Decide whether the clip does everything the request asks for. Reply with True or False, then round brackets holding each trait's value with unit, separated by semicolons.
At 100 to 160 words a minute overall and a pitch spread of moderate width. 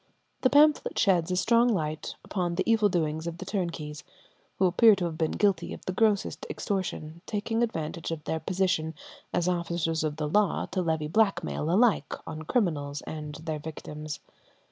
False (170 wpm; 4.2 semitones)